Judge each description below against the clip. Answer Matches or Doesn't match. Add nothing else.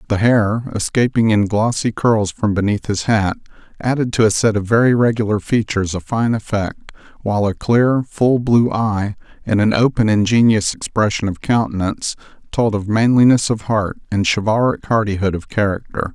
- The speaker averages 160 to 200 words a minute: Matches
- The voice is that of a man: Matches